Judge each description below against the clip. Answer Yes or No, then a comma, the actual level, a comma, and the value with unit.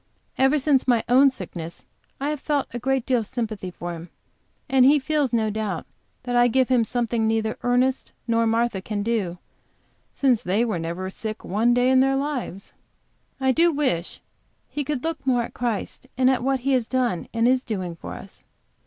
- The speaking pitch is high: Yes, high, 240 Hz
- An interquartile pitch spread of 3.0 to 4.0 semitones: Yes, average, 3.5 semitones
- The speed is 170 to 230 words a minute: Yes, average, 190 wpm